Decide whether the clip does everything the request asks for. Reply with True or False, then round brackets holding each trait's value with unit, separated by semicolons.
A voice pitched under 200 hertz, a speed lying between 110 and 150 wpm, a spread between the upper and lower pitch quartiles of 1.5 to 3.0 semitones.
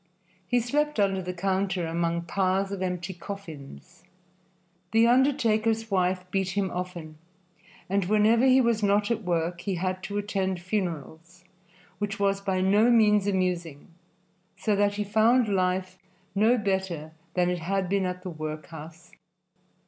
True (190 Hz; 145 wpm; 2.7 semitones)